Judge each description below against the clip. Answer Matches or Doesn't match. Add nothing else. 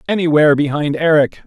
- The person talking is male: Matches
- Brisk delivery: Doesn't match